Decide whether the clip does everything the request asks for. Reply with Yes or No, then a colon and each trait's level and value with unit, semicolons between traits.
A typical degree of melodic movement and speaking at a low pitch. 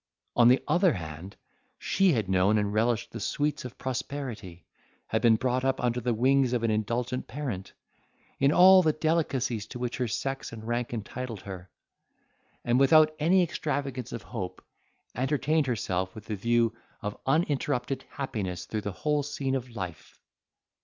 Yes: average, 4.4 semitones; low, 125 Hz